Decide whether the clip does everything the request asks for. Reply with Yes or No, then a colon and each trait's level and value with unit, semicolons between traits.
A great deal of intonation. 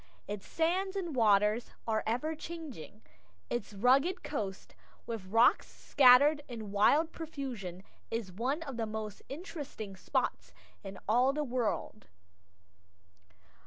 Yes: wide, 6.1 semitones